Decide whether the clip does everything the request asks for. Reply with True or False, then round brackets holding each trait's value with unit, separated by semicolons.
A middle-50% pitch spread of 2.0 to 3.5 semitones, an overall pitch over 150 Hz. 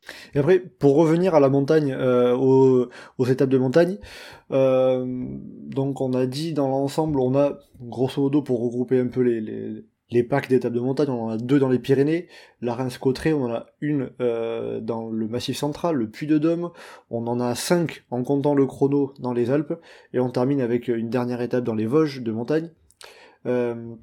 False (2.7 semitones; 130 Hz)